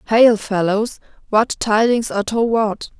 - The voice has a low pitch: No, high, 220 Hz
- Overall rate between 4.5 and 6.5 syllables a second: No, 4.2 syllables/s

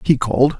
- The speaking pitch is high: No, low, 130 Hz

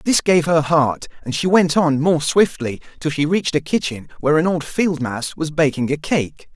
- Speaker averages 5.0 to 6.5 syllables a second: Yes, 5.1 syllables/s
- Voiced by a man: Yes, male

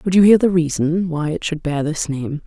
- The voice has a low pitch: No, medium, 165 Hz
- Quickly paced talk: Yes, fast, 265 wpm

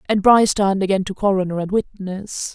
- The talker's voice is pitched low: No, high, 195 Hz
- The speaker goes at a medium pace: Yes, average, 190 wpm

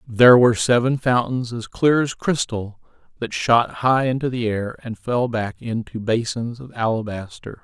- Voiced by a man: Yes, male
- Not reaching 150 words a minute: No, average, 165 wpm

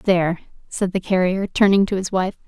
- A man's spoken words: No, female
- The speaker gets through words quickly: No, average, 195 wpm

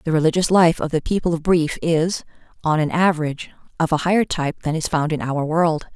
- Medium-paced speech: No, fast, 220 wpm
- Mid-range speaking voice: Yes, medium, 160 Hz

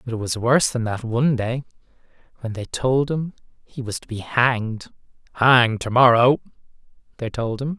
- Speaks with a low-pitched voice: Yes, low, 120 Hz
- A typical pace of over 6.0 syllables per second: No, 5.2 syllables/s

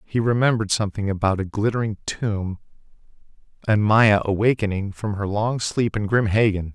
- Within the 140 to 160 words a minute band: Yes, average, 150 wpm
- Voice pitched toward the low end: Yes, low, 105 Hz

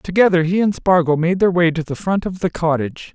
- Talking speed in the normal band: No, fast, 250 wpm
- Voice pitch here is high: No, medium, 175 Hz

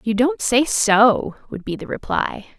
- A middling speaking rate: Yes, average, 185 wpm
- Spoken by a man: No, female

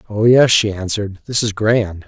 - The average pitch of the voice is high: No, low, 105 Hz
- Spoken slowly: No, average, 200 wpm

